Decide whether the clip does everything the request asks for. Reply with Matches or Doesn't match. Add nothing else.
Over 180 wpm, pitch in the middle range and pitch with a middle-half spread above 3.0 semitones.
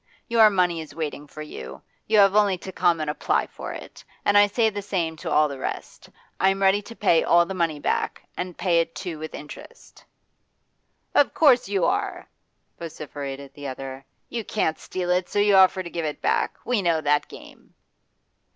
Matches